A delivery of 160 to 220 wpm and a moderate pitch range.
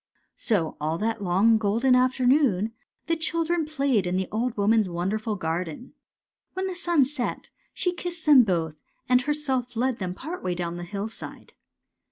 No: average, 170 wpm; wide, 7.1 semitones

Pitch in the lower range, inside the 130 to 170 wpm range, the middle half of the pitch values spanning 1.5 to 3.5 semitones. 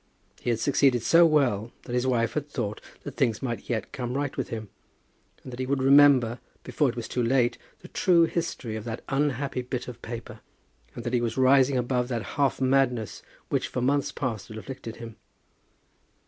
No: low, 125 Hz; average, 190 wpm; narrow, 2.6 semitones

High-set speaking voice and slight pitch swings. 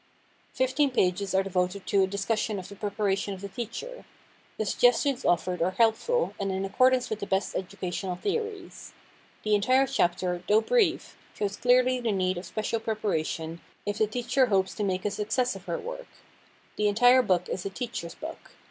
No: high, 210 Hz; average, 4.7 semitones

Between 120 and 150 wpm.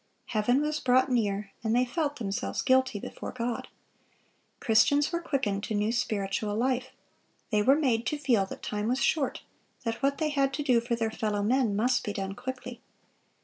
No: average, 185 wpm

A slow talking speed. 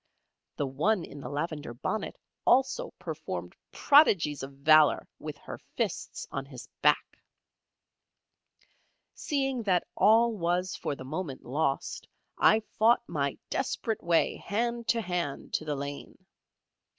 Yes: slow, 125 wpm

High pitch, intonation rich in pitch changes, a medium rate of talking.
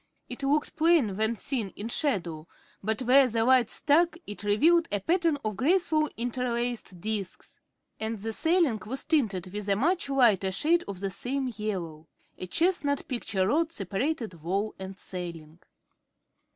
Yes: high, 230 Hz; wide, 6.7 semitones; average, 150 wpm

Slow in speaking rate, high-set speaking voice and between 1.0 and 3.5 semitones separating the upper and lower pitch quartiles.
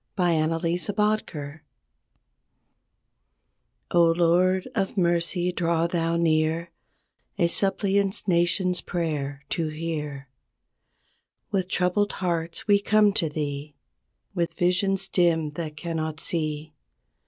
No: slow, 100 wpm; medium, 170 Hz; average, 2.7 semitones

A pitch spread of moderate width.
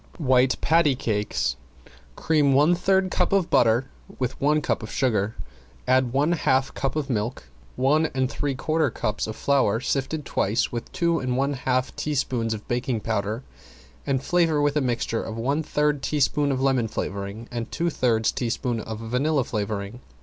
Yes: average, 4.4 semitones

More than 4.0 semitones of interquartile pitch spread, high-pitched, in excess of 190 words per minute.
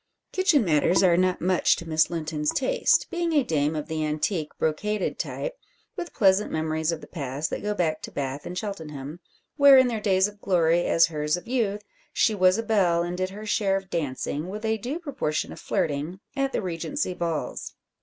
No: average, 5.2 semitones; medium, 180 Hz; average, 200 wpm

